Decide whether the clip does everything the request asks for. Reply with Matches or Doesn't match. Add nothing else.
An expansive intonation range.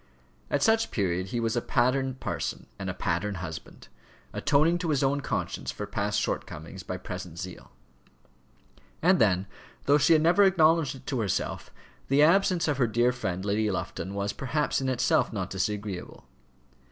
Matches